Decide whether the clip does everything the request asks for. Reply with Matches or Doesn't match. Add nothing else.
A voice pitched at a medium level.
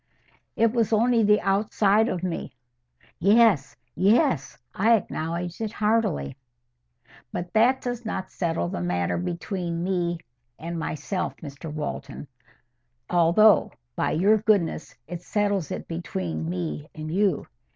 Matches